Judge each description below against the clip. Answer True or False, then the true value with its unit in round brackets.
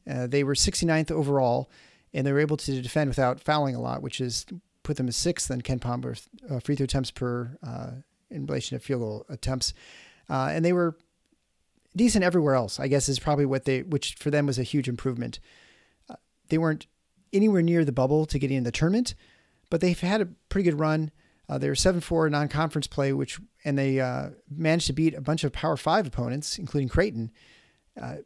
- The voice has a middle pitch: True (145 Hz)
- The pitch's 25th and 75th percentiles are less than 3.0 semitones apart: False (3.7 semitones)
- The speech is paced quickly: True (210 wpm)